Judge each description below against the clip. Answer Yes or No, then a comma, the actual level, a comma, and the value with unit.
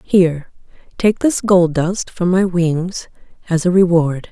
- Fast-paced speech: No, average, 155 wpm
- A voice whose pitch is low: No, medium, 175 Hz